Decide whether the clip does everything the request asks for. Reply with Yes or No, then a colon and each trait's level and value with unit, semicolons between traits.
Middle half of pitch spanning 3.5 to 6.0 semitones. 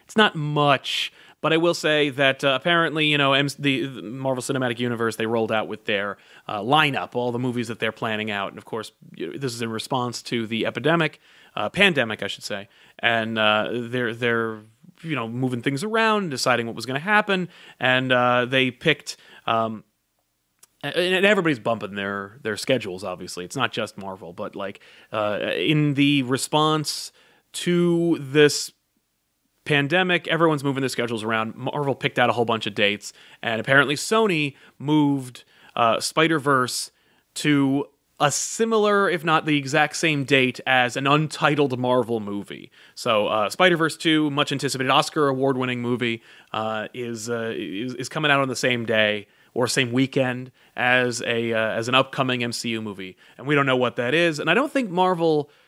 Yes: average, 4.5 semitones